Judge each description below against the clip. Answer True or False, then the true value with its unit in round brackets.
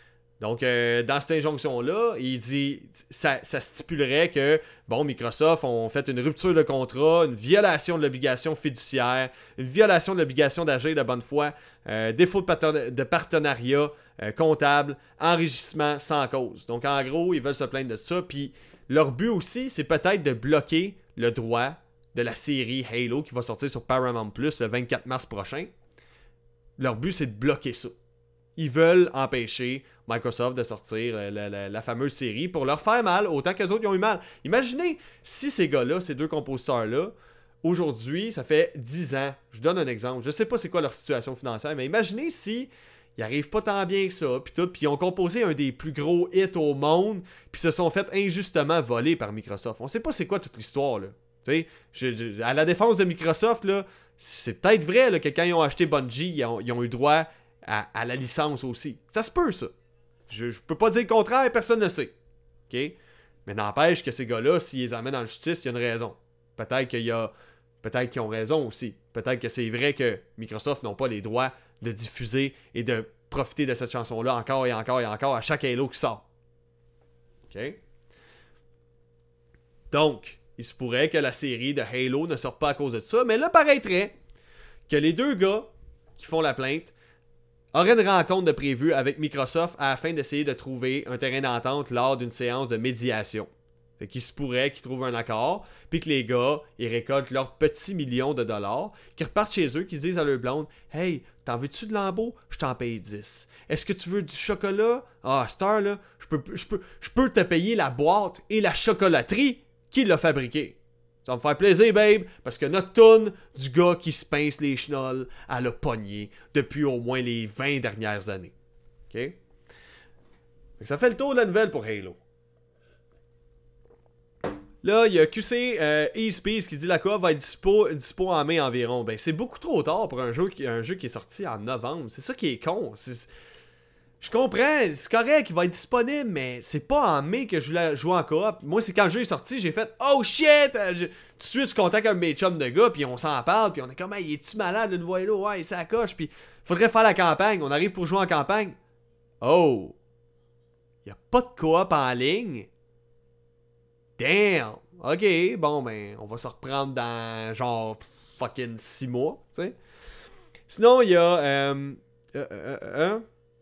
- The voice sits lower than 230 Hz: True (140 Hz)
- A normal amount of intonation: False (6.8 semitones)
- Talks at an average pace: True (200 wpm)